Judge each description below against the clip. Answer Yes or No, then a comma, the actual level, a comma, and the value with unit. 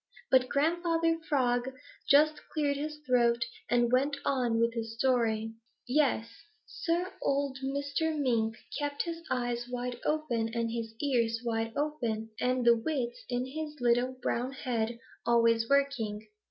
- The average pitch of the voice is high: Yes, very high, 250 Hz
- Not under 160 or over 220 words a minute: No, average, 140 wpm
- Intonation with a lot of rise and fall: No, average, 3.5 semitones